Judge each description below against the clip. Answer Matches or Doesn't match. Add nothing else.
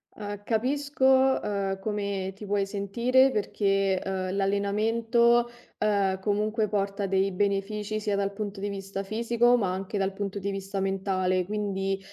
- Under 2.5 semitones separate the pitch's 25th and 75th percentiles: Matches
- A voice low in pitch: Doesn't match